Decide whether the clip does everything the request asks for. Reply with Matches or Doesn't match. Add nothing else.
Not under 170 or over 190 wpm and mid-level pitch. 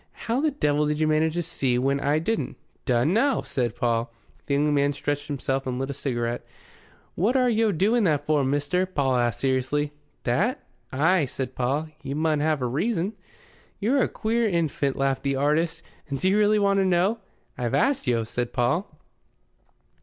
Matches